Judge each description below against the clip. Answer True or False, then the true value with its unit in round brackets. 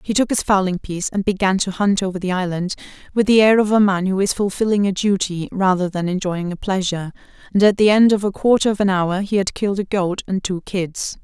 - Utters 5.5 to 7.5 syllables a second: True (5.9 syllables/s)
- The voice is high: True (195 Hz)